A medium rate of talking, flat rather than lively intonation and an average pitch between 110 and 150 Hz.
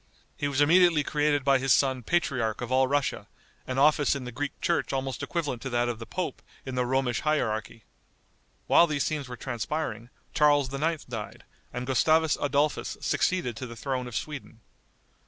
No: average, 175 wpm; average, 3.4 semitones; low, 135 Hz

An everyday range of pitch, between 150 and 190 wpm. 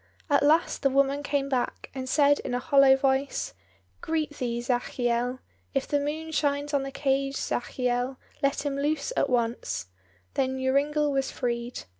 No: narrow, 2.3 semitones; average, 160 wpm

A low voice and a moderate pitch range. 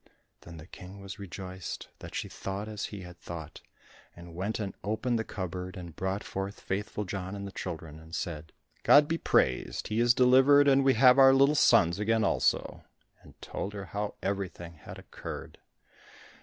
Yes: low, 100 Hz; average, 4.0 semitones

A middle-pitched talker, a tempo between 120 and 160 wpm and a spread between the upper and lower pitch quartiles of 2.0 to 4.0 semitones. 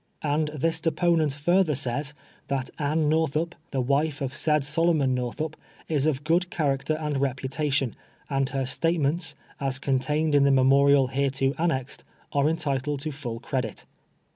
Yes: medium, 145 Hz; average, 145 wpm; narrow, 2.6 semitones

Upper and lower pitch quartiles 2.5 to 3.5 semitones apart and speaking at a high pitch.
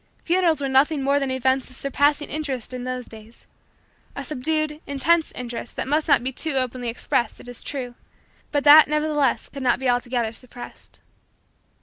Yes: average, 3.2 semitones; very high, 265 Hz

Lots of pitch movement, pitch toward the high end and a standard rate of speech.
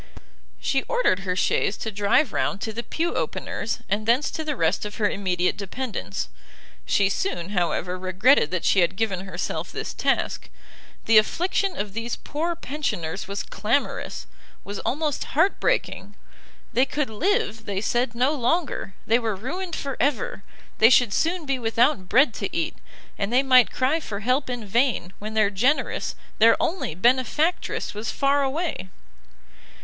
Yes: wide, 5.9 semitones; high, 230 Hz; average, 160 wpm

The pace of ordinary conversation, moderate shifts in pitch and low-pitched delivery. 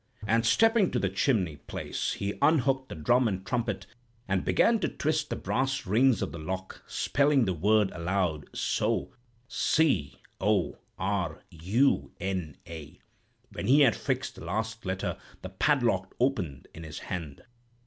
No: average, 150 wpm; wide, 6.1 semitones; low, 100 Hz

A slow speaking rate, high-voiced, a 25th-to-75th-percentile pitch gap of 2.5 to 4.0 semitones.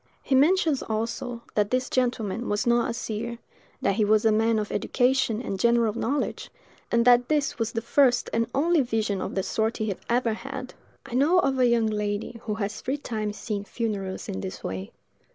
No: average, 195 wpm; high, 230 Hz; average, 2.9 semitones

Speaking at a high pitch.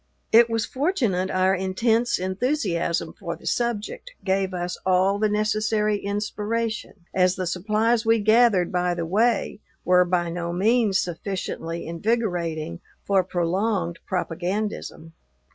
Yes: high, 195 Hz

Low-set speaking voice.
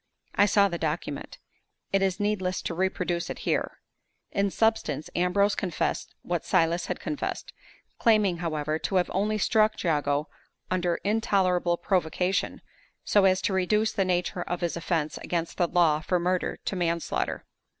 No: medium, 180 Hz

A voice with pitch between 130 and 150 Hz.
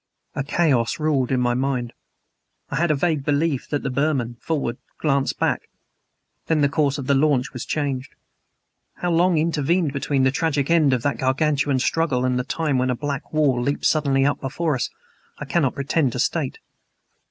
Yes: medium, 140 Hz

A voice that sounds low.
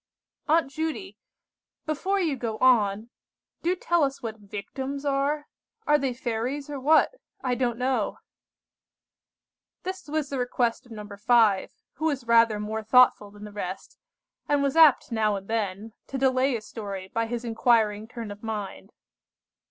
No: high, 240 Hz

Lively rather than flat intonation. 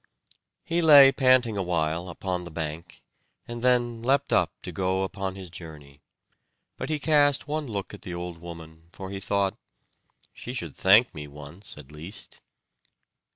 Yes: wide, 6.5 semitones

